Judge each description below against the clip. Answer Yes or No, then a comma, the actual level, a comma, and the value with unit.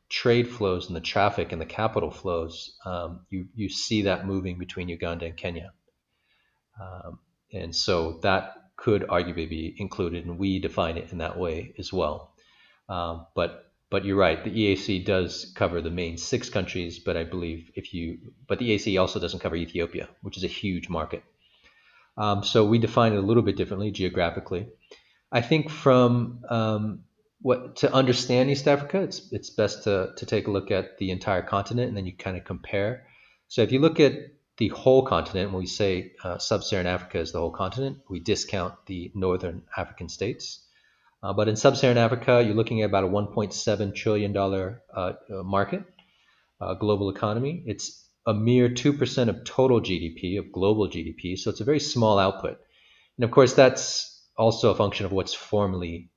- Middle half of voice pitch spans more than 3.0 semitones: Yes, average, 4.5 semitones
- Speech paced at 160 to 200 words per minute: Yes, average, 185 wpm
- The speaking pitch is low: Yes, low, 100 Hz